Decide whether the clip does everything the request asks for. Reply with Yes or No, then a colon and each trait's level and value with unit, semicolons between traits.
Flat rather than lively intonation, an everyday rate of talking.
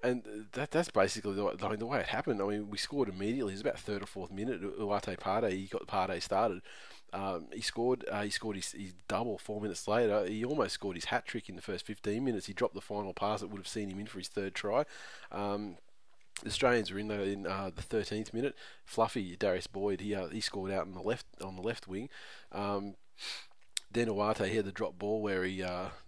No: narrow, 1.7 semitones; fast, 235 wpm